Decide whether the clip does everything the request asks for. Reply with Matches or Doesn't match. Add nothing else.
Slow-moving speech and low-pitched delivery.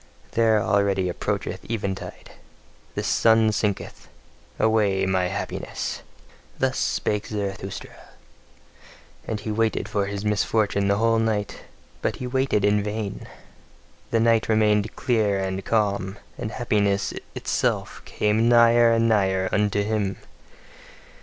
Matches